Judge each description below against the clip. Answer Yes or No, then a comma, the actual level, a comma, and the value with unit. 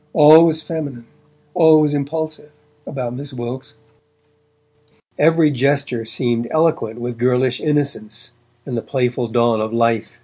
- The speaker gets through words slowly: Yes, slow, 130 wpm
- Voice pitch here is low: Yes, low, 130 Hz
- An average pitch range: Yes, average, 4.1 semitones